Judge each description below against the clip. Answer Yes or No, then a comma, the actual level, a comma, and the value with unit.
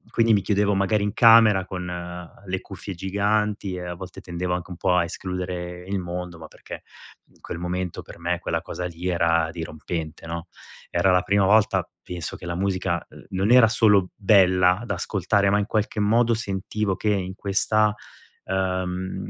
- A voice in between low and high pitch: No, very low, 95 Hz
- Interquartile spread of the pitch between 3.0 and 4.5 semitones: No, narrow, 2.5 semitones